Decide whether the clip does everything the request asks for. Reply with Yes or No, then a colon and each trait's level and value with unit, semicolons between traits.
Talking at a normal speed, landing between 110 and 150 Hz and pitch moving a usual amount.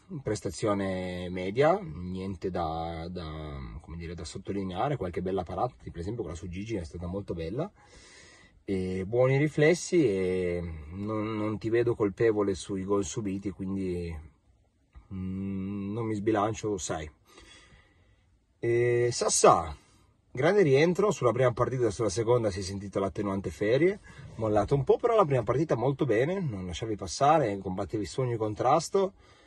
No: average, 145 wpm; low, 100 Hz; average, 4.4 semitones